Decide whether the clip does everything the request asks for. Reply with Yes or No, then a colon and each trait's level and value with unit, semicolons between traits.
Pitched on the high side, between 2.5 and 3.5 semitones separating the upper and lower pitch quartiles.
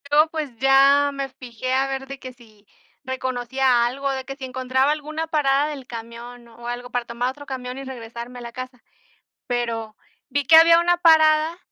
Yes: very high, 260 Hz; average, 2.8 semitones